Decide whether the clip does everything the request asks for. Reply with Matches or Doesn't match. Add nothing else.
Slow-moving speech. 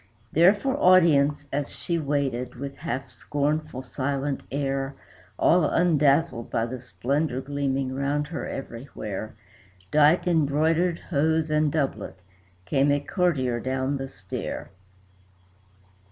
Matches